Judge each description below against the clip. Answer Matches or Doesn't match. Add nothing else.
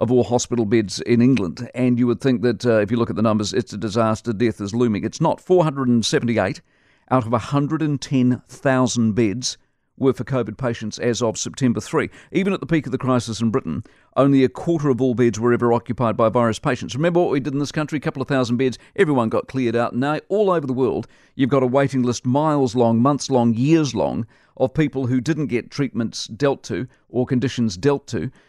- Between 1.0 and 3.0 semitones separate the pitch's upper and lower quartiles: Matches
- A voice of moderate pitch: Doesn't match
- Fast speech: Matches